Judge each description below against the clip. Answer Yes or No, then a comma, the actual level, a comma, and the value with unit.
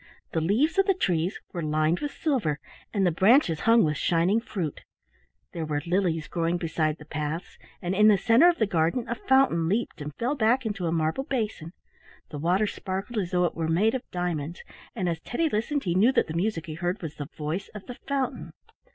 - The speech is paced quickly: Yes, fast, 210 wpm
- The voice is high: No, medium, 180 Hz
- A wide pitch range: Yes, wide, 5.8 semitones